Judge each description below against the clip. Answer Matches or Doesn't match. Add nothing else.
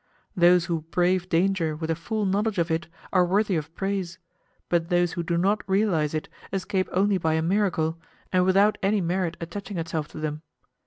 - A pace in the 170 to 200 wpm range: Matches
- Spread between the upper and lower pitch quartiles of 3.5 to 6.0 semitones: Doesn't match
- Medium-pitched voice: Matches